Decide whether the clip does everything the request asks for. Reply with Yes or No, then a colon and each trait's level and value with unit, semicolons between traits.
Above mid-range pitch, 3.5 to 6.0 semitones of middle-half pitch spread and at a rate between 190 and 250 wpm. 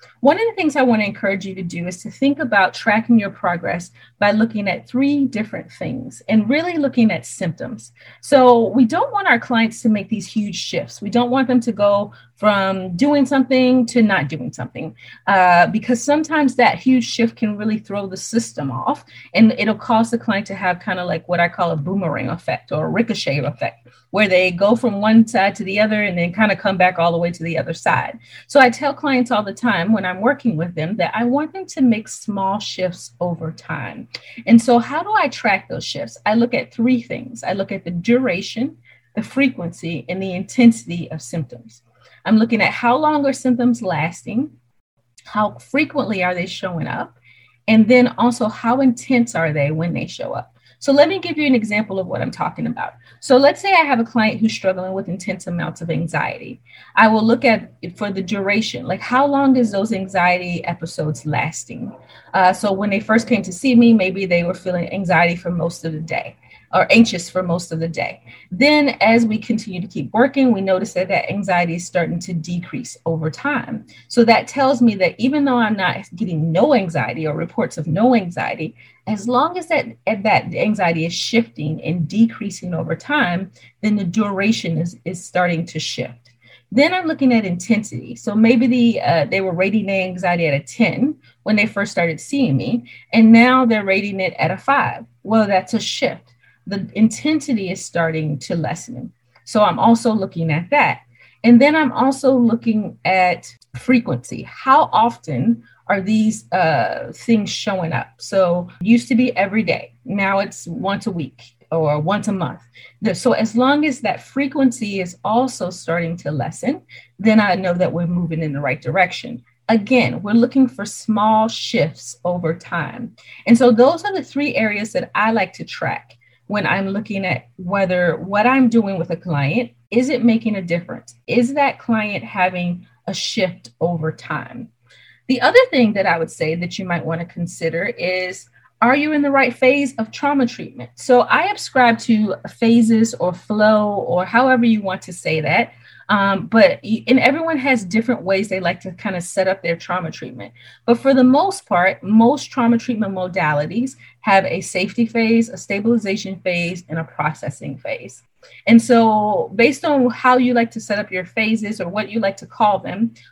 Yes: high, 205 Hz; wide, 5.5 semitones; average, 200 wpm